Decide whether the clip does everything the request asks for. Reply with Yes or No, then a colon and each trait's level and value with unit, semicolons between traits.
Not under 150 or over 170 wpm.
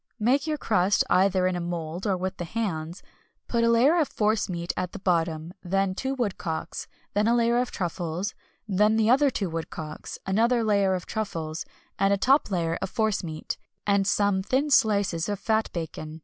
No: average, 190 wpm